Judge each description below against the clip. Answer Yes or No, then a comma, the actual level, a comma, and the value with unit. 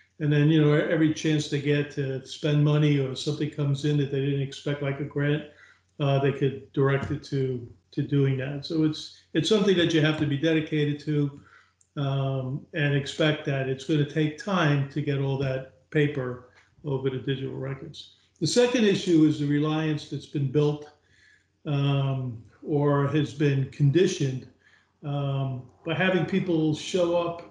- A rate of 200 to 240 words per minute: No, average, 175 wpm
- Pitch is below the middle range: No, medium, 145 Hz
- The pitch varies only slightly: Yes, narrow, 2.0 semitones